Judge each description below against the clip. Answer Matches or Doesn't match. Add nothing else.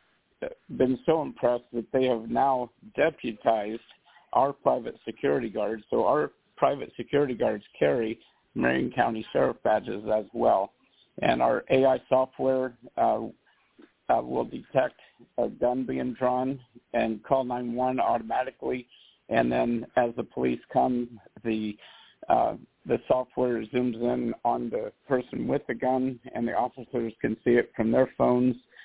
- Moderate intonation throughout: Doesn't match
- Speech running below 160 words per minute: Matches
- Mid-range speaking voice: Doesn't match